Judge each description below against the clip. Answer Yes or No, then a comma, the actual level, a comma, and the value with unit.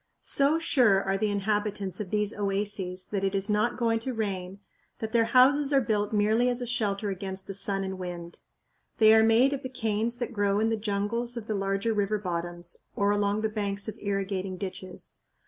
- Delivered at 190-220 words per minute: Yes, average, 200 wpm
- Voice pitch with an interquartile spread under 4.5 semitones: Yes, narrow, 2.6 semitones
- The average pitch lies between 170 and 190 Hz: No, high, 205 Hz